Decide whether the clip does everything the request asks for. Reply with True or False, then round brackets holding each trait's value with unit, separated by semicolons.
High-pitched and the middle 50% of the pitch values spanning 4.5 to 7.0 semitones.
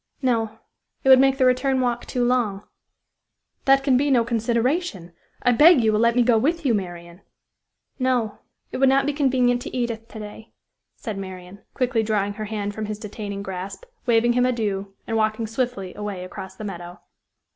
False (225 Hz; 3.7 semitones)